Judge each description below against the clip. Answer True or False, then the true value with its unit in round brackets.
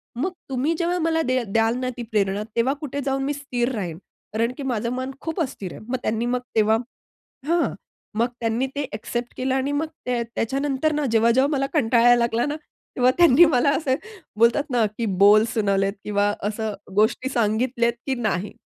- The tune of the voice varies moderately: True (3.6 semitones)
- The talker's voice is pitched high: True (245 Hz)